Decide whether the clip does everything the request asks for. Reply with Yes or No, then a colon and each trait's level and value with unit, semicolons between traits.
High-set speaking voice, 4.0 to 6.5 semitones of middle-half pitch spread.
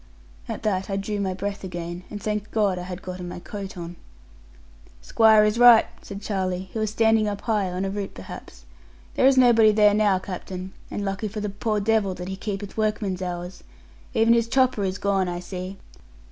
No: high, 200 Hz; narrow, 2.5 semitones